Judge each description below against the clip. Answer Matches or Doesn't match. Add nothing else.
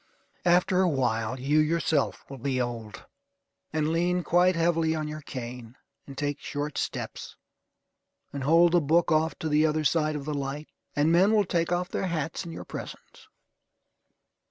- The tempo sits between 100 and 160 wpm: Doesn't match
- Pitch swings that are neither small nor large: Matches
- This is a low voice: Doesn't match